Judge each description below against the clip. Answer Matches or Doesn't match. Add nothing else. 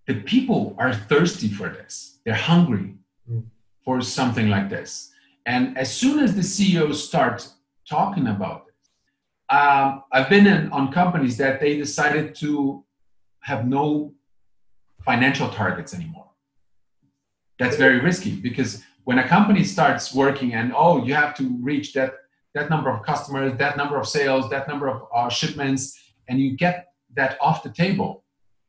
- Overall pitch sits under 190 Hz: Matches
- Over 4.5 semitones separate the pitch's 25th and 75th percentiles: Doesn't match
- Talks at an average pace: Doesn't match